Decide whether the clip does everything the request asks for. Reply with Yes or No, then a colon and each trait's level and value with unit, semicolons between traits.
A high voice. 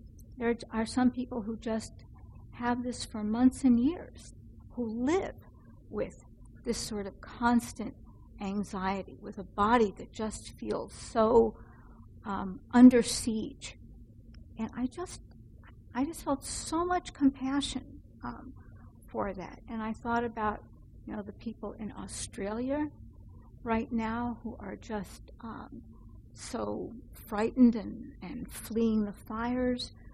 Yes: high, 235 Hz